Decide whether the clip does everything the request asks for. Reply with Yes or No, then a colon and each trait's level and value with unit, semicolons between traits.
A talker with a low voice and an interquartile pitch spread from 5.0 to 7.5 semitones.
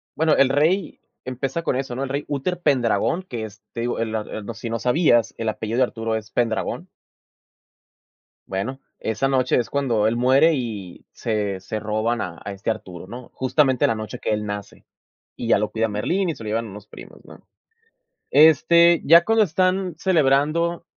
Yes: low, 120 Hz; wide, 5.6 semitones